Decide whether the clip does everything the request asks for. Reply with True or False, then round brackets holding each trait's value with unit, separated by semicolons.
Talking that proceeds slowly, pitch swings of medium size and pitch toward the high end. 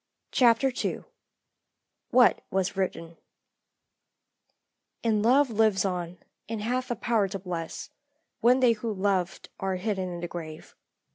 True (130 wpm; 4.4 semitones; 200 Hz)